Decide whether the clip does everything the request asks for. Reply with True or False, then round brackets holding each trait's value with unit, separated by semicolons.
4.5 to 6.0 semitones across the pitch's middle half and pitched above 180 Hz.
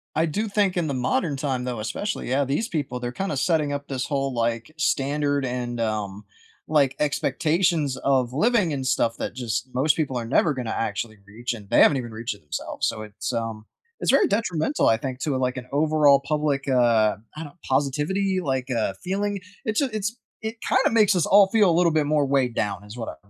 False (4.8 semitones; 140 Hz)